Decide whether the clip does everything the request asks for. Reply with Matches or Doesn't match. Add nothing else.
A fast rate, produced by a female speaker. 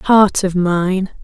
Doesn't match